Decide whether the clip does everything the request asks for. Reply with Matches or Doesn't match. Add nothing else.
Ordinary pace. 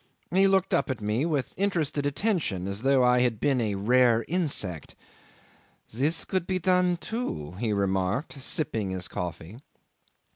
Matches